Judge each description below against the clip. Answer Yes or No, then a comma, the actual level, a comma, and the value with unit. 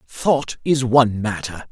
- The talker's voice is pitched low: Yes, low, 120 Hz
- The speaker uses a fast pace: No, average, 140 wpm